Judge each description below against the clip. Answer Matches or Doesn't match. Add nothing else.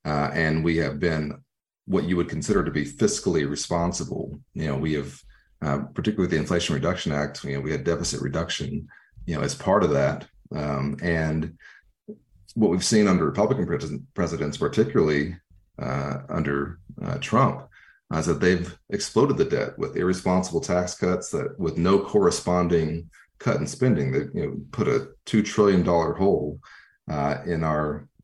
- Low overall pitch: Matches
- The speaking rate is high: Doesn't match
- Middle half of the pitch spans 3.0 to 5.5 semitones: Matches